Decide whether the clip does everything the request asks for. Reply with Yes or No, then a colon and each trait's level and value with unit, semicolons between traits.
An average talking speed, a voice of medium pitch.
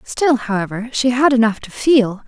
No: average, 185 wpm; high, 235 Hz